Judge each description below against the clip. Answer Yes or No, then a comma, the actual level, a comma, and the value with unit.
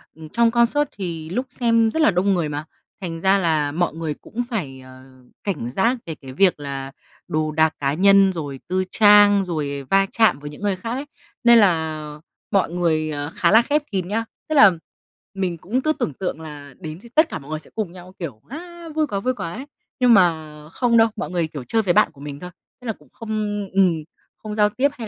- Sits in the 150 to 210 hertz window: Yes, medium, 185 Hz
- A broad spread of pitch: Yes, wide, 6.4 semitones